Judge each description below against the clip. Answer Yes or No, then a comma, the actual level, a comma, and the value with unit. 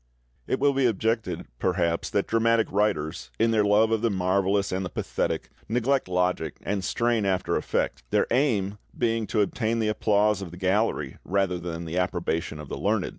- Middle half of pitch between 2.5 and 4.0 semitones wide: Yes, average, 3.7 semitones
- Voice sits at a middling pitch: No, low, 100 Hz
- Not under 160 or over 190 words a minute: Yes, average, 180 wpm